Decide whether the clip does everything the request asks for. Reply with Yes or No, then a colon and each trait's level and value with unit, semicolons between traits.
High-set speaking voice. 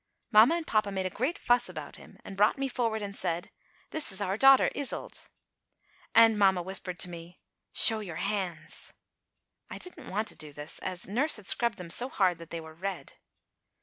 Yes: high, 200 Hz